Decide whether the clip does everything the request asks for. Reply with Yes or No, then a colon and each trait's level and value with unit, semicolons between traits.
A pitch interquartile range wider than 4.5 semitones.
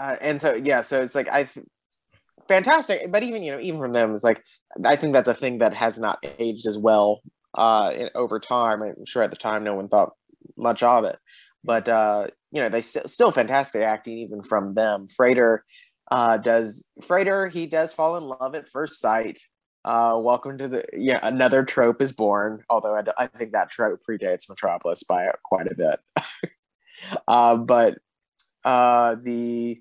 No: average, 3.9 semitones